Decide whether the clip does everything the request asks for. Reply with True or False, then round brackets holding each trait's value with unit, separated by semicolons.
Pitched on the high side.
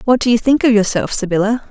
True (225 Hz)